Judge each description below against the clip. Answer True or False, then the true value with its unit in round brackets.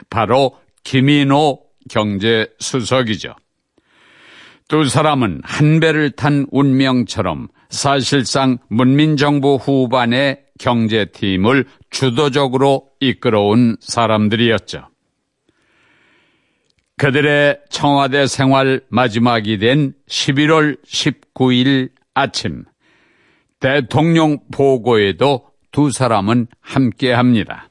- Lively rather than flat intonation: False (3.1 semitones)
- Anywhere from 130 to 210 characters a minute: True (185 characters per minute)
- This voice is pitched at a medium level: False (130 Hz)